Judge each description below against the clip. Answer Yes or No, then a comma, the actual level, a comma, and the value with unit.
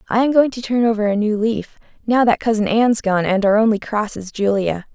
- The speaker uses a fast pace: Yes, fast, 245 wpm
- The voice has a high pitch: Yes, high, 215 Hz